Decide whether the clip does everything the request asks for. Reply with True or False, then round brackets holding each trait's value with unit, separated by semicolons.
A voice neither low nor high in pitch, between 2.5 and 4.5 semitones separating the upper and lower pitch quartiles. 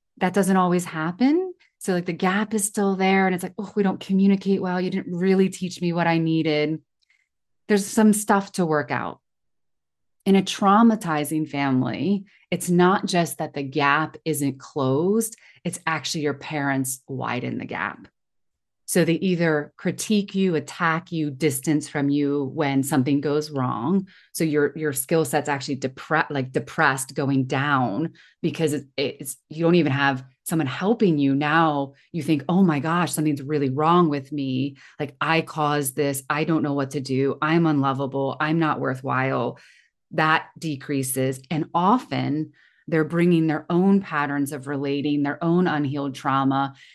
True (155 Hz; 4.1 semitones)